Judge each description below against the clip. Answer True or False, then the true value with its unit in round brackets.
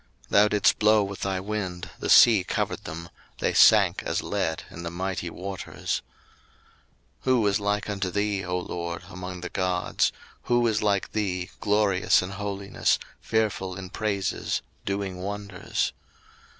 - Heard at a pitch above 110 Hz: False (100 Hz)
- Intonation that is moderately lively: False (2.2 semitones)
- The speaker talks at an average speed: True (150 wpm)